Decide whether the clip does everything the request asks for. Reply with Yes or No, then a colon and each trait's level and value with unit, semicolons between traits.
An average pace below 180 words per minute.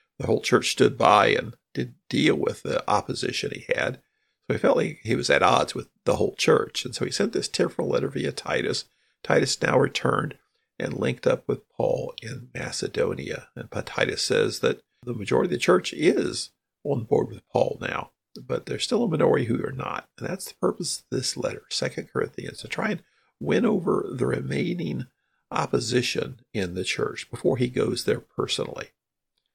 No: average, 185 wpm